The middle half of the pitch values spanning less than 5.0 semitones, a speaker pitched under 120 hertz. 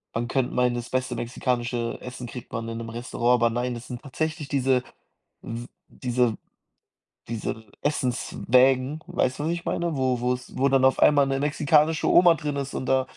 No: narrow, 2.6 semitones; low, 130 Hz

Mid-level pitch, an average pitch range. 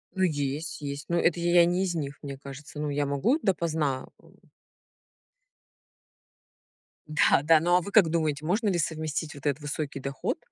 Yes: medium, 155 Hz; average, 3.3 semitones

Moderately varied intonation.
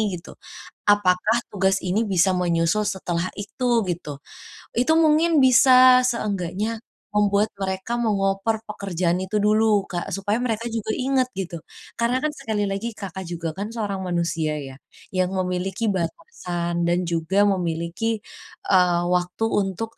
Yes: average, 3.5 semitones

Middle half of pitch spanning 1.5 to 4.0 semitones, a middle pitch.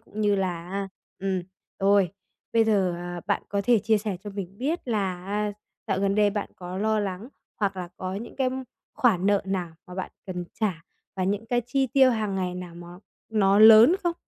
No: average, 2.7 semitones; high, 200 Hz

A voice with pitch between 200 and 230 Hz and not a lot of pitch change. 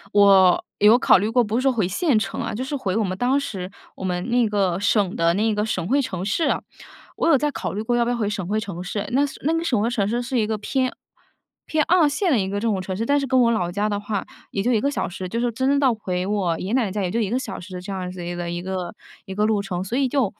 No: high, 210 Hz; average, 4.5 semitones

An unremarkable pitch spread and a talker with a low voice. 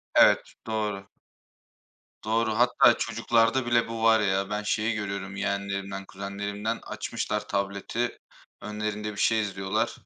No: narrow, 2.3 semitones; low, 105 Hz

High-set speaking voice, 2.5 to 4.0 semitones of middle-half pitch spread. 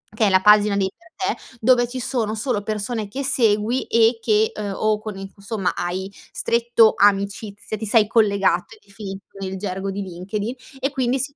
Yes: high, 215 Hz; average, 2.8 semitones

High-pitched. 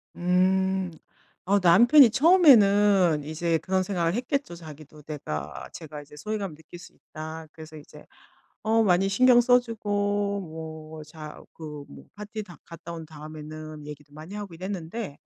No: medium, 175 Hz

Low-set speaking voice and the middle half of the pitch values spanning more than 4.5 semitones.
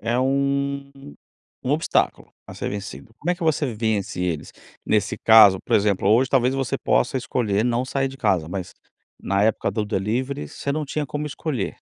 Yes: low, 120 Hz; average, 5.2 semitones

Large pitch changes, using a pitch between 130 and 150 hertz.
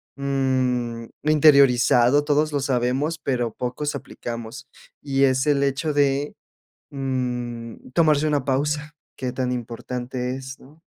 No: average, 2.7 semitones; low, 135 Hz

